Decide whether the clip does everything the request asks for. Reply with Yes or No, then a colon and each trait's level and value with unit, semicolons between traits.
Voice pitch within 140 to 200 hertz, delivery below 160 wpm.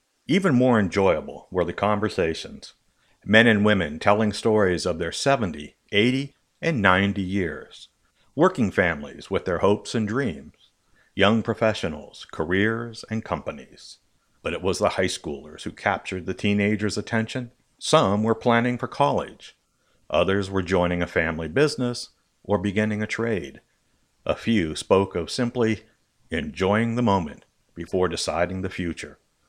No: low, 105 Hz; average, 140 wpm